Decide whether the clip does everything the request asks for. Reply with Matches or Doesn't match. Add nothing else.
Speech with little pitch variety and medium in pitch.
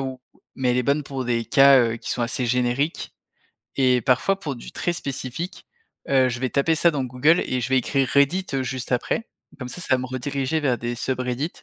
Doesn't match